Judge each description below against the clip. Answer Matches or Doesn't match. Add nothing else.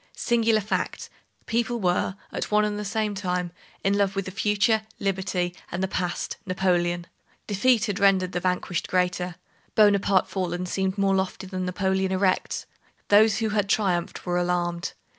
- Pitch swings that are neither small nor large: Doesn't match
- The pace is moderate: Matches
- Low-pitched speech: Doesn't match